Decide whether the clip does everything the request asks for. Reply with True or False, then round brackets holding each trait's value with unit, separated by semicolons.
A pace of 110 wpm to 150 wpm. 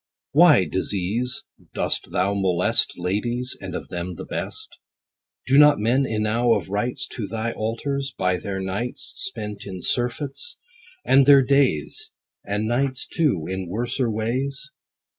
True (140 wpm)